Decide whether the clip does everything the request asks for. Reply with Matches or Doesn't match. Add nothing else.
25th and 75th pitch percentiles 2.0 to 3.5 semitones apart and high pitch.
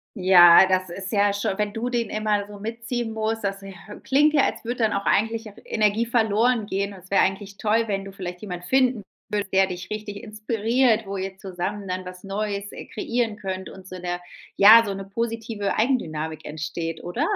Matches